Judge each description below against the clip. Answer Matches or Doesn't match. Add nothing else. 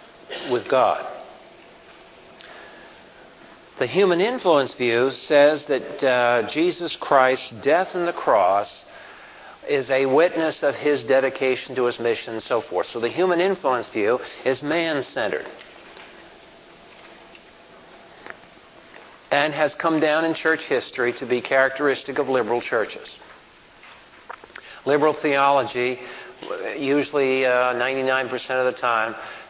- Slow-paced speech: Matches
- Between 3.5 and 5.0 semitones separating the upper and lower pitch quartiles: Doesn't match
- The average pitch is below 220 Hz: Matches